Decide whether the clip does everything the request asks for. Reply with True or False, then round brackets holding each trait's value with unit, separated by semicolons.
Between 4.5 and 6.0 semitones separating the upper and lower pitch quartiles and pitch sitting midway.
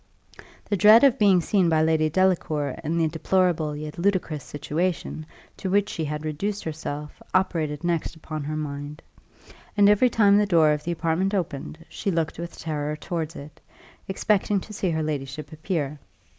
False (3.7 semitones; 160 Hz)